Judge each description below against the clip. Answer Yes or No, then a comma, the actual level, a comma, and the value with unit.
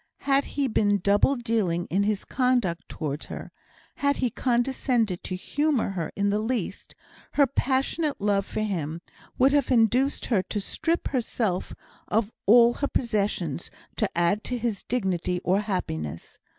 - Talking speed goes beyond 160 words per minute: No, average, 150 wpm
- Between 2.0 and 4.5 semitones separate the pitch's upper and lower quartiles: No, average, 5.3 semitones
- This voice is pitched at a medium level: No, high, 215 Hz